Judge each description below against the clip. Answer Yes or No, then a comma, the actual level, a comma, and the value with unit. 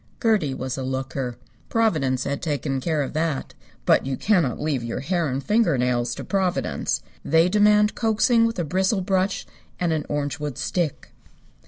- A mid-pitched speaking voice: Yes, medium, 155 Hz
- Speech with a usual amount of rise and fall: No, wide, 6.3 semitones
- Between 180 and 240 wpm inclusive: No, average, 165 wpm